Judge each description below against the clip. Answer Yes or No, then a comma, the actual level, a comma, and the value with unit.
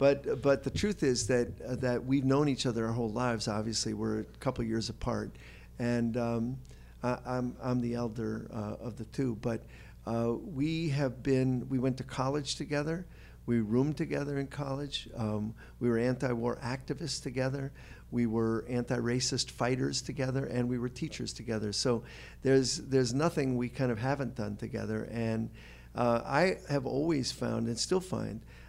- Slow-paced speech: No, average, 175 wpm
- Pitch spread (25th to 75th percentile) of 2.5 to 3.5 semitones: Yes, average, 2.9 semitones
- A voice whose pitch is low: Yes, low, 125 Hz